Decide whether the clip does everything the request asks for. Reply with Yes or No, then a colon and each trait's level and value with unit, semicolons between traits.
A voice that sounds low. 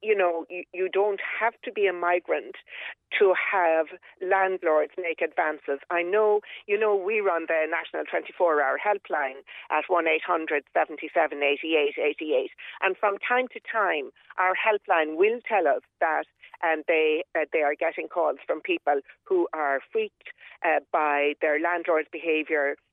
No: medium, 185 Hz